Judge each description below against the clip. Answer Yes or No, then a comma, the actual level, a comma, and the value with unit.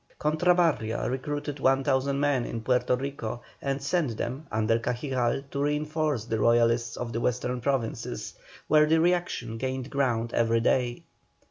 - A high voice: No, low, 130 Hz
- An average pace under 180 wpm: Yes, average, 140 wpm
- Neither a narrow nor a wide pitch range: Yes, average, 3.6 semitones